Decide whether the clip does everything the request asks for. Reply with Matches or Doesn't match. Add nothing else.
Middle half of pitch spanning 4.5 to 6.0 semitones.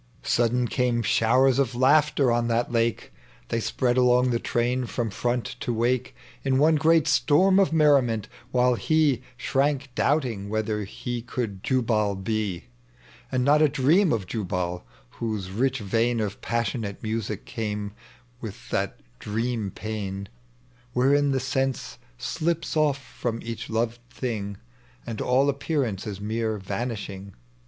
Doesn't match